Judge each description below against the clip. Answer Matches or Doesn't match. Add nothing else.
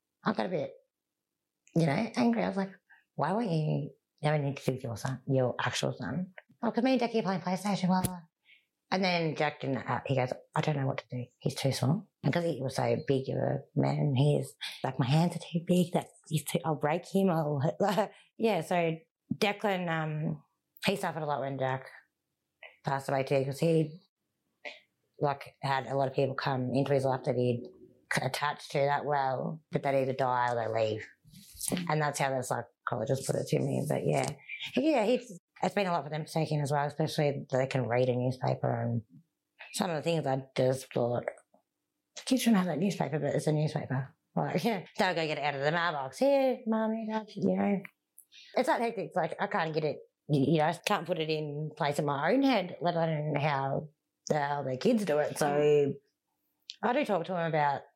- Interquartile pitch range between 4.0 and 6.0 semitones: Matches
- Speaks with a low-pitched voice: Doesn't match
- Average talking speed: Doesn't match